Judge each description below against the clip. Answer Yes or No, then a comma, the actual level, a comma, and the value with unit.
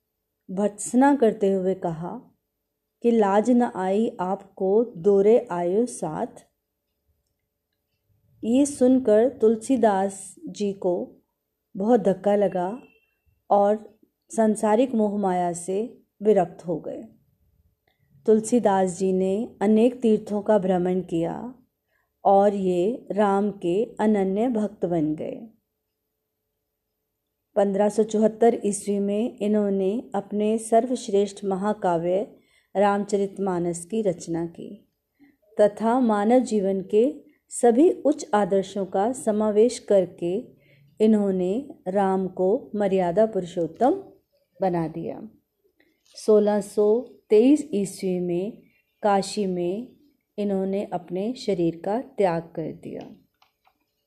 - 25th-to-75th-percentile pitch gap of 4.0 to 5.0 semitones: No, average, 3.0 semitones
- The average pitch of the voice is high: Yes, high, 205 Hz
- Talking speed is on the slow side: Yes, slow, 95 wpm